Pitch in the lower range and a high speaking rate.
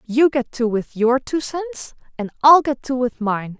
No: very high, 255 Hz; fast, 215 wpm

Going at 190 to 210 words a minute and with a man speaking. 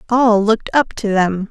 No: average, 200 wpm; female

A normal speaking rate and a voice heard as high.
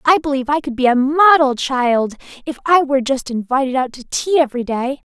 No: fast, 210 wpm; very high, 270 Hz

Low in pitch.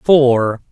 Yes: low, 130 Hz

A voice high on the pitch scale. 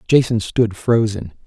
No: low, 110 Hz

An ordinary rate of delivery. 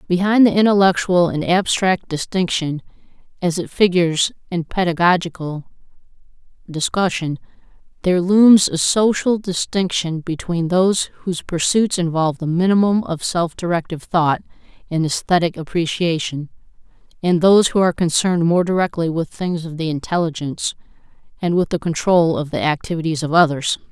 No: slow, 130 wpm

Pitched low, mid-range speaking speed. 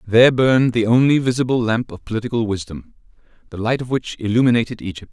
Yes: low, 115 Hz; average, 175 wpm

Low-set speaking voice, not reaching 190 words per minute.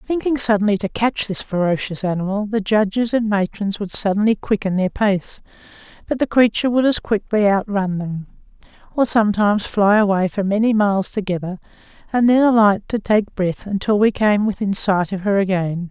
No: high, 205 Hz; average, 175 wpm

